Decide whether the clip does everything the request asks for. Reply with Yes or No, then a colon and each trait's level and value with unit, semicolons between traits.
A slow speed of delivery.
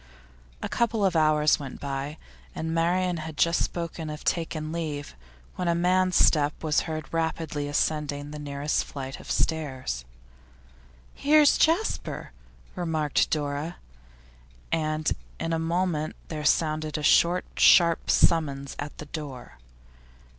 Yes: slow, 130 wpm